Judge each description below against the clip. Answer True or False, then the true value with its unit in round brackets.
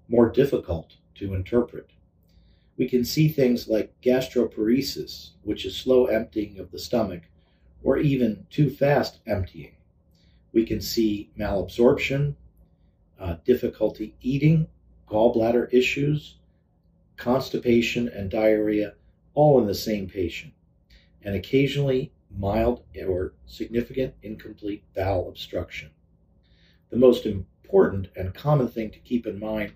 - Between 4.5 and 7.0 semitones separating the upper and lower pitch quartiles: True (5.6 semitones)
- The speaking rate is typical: False (115 wpm)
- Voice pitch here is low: True (105 Hz)